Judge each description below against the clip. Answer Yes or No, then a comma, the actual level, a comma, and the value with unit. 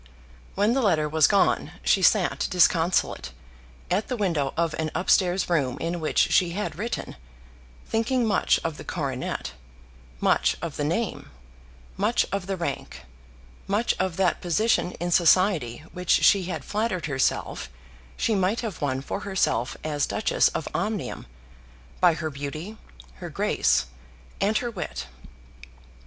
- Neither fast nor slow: Yes, average, 145 wpm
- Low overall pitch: No, medium, 175 Hz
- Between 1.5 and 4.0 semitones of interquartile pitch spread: No, average, 4.5 semitones